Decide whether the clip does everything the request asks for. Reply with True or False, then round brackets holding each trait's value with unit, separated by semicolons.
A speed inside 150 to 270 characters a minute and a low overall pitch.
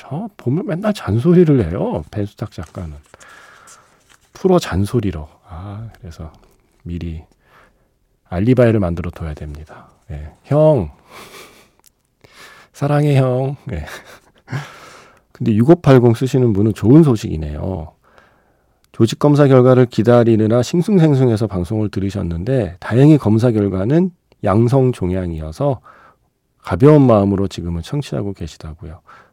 True (255 characters per minute; 110 Hz)